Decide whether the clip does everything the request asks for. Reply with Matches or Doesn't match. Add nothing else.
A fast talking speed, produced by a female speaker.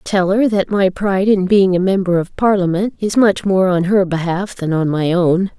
Matches